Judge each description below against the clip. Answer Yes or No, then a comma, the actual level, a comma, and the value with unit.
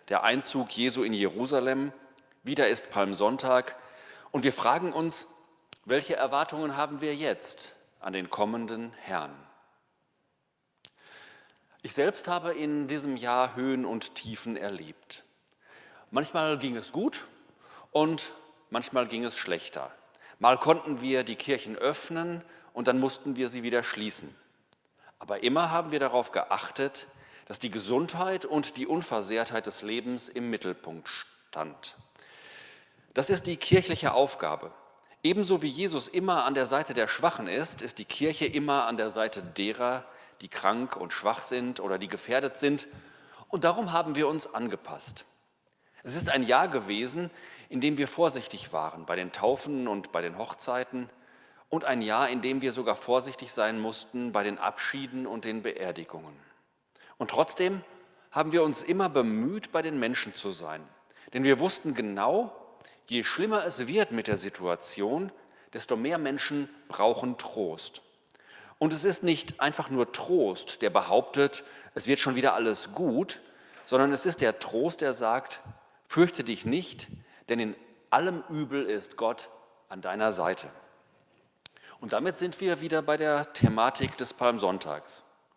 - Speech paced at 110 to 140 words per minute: No, average, 150 wpm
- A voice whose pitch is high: No, low, 135 Hz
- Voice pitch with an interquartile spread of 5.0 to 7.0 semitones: Yes, average, 5.3 semitones